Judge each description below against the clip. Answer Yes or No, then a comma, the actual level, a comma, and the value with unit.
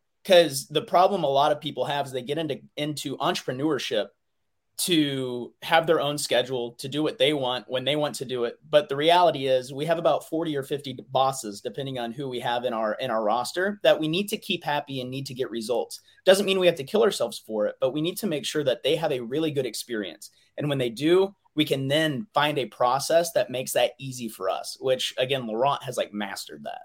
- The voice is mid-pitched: Yes, medium, 145 Hz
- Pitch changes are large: No, average, 5.0 semitones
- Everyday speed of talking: No, fast, 240 wpm